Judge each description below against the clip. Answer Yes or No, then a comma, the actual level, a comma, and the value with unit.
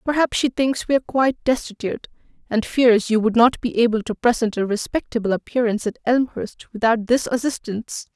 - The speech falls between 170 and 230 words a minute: Yes, average, 175 wpm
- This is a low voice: No, high, 235 Hz